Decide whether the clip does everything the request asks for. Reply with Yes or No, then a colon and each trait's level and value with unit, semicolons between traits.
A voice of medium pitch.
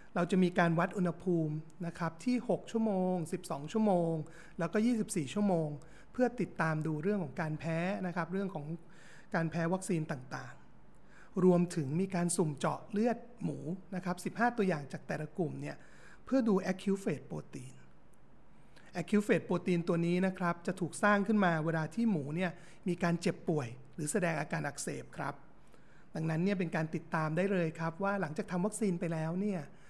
Yes: medium, 175 Hz